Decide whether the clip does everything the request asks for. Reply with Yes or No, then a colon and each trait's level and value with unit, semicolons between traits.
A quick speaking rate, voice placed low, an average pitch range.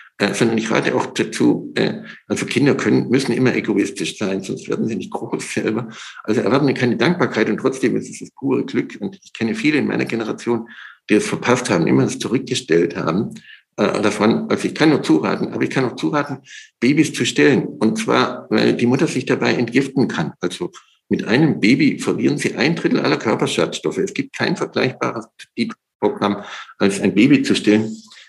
Yes: fast, 195 wpm; low, 120 Hz; average, 3.0 semitones